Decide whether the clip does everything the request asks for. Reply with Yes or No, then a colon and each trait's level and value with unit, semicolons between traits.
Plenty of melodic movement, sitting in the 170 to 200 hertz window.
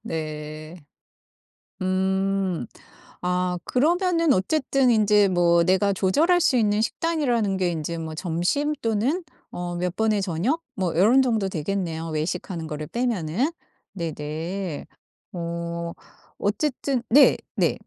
Yes: wide, 5.8 semitones; high, 190 Hz